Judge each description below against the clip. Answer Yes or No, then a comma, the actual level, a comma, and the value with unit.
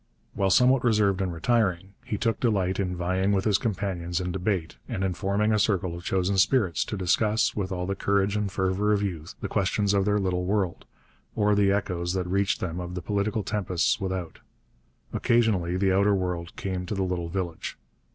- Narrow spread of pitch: Yes, narrow, 2.3 semitones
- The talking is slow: No, average, 195 wpm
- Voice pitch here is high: No, very low, 95 Hz